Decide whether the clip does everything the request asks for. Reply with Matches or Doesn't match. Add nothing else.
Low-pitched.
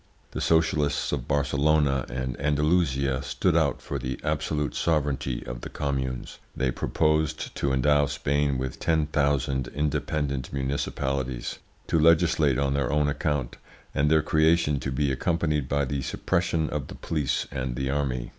Matches